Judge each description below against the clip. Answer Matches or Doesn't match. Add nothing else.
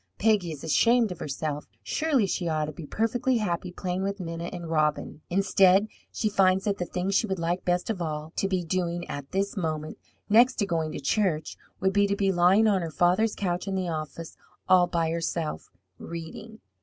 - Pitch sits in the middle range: Matches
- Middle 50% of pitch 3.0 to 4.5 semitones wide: Matches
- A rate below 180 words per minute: Doesn't match